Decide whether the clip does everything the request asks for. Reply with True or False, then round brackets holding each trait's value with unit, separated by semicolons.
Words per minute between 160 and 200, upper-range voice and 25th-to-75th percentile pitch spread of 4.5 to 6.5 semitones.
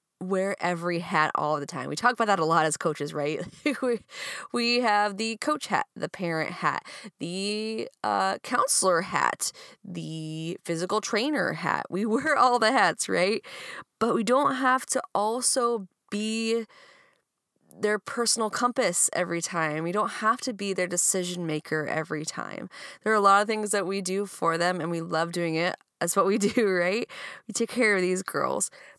True (180 wpm; 200 Hz; 5.6 semitones)